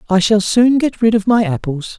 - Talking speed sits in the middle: No, fast, 240 wpm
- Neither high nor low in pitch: No, high, 210 Hz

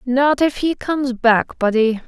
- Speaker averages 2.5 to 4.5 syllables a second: Yes, 4.2 syllables/s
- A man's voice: No, female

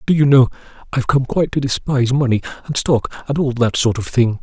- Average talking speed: No, fast, 230 wpm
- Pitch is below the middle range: Yes, low, 130 Hz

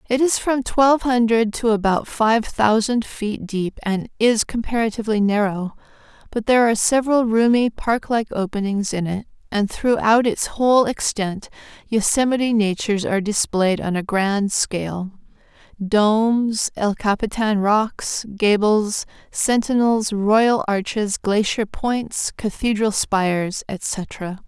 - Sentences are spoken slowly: Yes, slow, 125 wpm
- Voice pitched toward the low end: No, high, 215 Hz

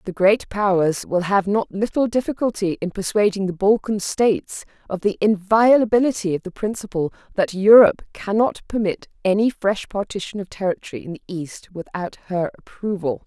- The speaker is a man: No, female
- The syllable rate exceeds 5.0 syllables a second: Yes, 5.2 syllables/s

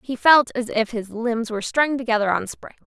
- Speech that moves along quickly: Yes, fast, 230 wpm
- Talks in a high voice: Yes, high, 235 Hz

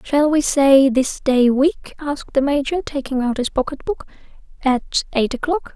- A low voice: No, very high, 280 Hz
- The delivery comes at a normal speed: Yes, average, 165 wpm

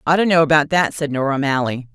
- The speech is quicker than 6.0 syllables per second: Yes, 6.7 syllables/s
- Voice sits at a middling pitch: Yes, medium, 150 Hz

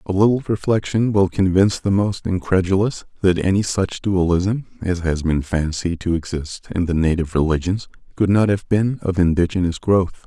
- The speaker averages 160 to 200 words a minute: Yes, average, 170 wpm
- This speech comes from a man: Yes, male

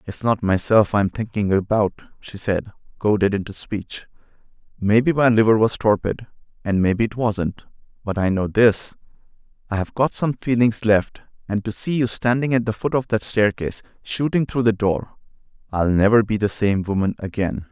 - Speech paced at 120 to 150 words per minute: No, average, 170 wpm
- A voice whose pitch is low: Yes, low, 105 Hz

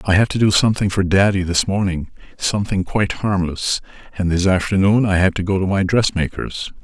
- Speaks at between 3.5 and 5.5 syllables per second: No, 5.7 syllables/s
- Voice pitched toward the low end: Yes, very low, 95 Hz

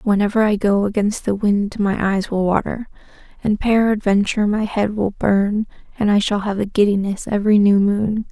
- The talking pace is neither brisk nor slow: Yes, average, 180 wpm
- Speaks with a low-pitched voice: No, high, 205 Hz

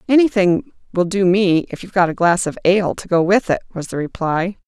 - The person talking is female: Yes, female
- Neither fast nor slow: No, fast, 230 wpm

